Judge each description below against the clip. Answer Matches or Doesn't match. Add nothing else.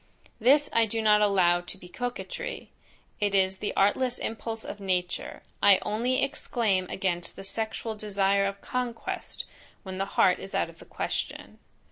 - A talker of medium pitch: Doesn't match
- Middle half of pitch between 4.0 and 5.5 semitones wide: Doesn't match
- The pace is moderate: Matches